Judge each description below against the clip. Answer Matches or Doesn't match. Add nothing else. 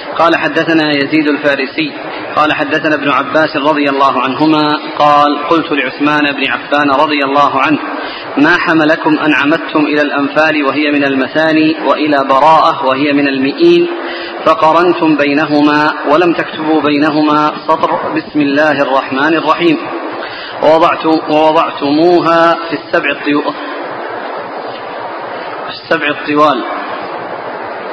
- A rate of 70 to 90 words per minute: Doesn't match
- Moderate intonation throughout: Doesn't match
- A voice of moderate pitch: Matches